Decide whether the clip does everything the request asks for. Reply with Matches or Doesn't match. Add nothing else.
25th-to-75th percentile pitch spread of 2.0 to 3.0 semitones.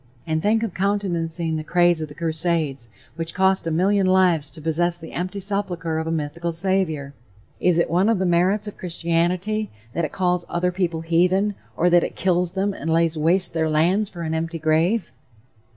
Matches